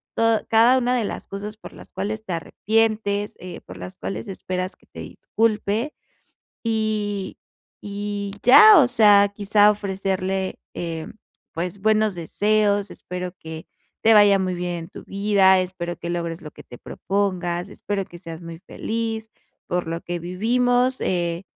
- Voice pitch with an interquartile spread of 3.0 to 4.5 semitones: Yes, average, 3.5 semitones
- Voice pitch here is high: Yes, high, 200 Hz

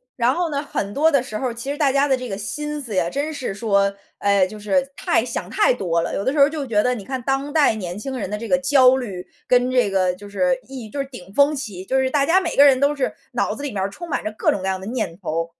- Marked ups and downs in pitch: Yes, wide, 5.7 semitones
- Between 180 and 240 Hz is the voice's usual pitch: No, very high, 255 Hz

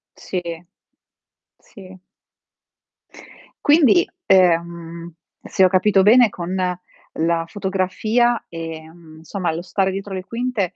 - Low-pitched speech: No, medium, 185 Hz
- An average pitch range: Yes, average, 3.2 semitones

